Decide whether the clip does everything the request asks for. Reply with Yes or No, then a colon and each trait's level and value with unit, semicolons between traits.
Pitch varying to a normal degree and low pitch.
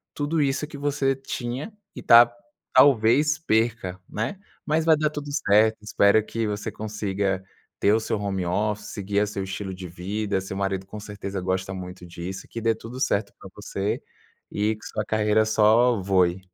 Yes: average, 3.7 semitones; low, 105 Hz